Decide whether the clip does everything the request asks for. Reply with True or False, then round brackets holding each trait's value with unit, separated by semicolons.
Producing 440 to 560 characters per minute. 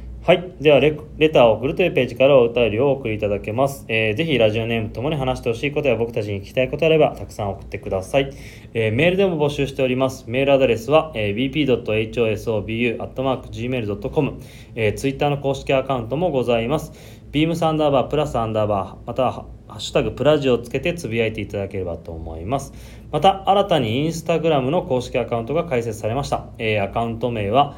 True (510 characters per minute)